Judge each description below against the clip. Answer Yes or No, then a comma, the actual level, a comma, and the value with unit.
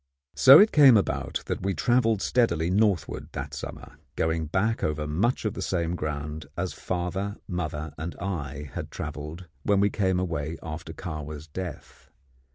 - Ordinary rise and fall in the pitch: Yes, average, 4.5 semitones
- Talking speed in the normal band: Yes, average, 160 wpm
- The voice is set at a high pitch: No, very low, 85 Hz